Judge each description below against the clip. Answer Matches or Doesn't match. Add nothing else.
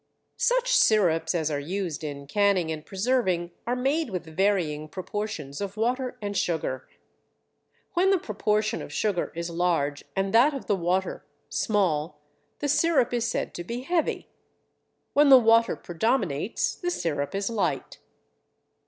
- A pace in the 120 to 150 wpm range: Matches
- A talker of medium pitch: Doesn't match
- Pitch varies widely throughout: Matches